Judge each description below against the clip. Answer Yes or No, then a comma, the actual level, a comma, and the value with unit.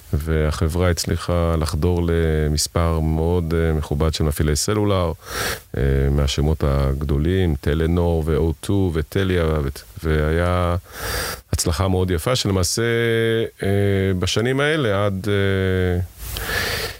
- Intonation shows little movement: No, average, 3.6 semitones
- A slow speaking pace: Yes, slow, 80 wpm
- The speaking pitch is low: Yes, very low, 85 Hz